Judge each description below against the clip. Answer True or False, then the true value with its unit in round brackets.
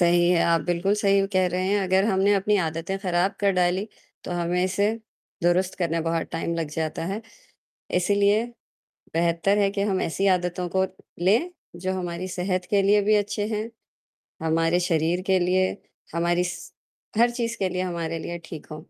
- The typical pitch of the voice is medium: True (180 Hz)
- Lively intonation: False (2.5 semitones)